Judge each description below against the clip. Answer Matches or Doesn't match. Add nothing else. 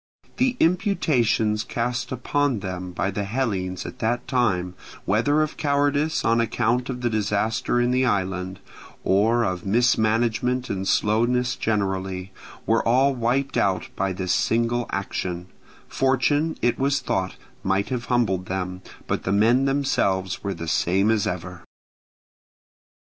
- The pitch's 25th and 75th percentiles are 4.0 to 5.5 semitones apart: Matches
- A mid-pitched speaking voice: Doesn't match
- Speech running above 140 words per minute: Doesn't match